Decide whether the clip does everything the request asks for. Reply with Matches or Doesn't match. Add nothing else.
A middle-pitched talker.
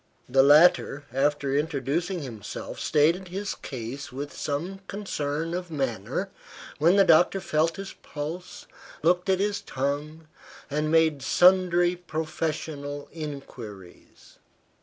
Matches